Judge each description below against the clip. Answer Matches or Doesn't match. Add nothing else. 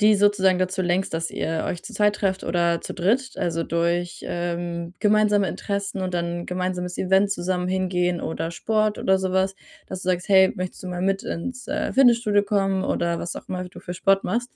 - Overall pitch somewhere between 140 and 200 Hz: Matches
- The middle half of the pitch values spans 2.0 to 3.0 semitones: Matches